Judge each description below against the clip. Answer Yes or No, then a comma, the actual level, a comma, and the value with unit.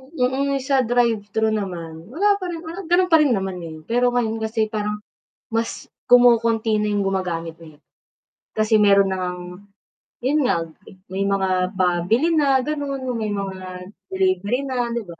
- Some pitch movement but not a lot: Yes, average, 5.0 semitones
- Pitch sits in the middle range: No, high, 215 Hz